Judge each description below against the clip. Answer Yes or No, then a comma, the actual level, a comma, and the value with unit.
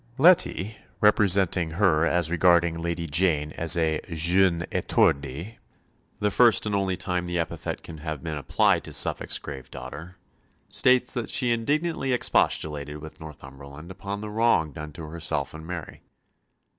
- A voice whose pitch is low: Yes, very low, 85 Hz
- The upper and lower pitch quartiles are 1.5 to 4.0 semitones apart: No, average, 4.4 semitones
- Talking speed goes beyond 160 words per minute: No, average, 145 wpm